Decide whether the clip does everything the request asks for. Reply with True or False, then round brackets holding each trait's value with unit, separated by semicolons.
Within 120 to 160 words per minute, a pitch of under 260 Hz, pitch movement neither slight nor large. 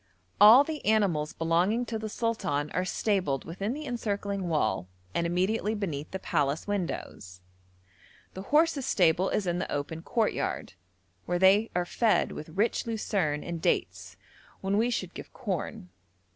True (150 wpm; 190 Hz; 5.0 semitones)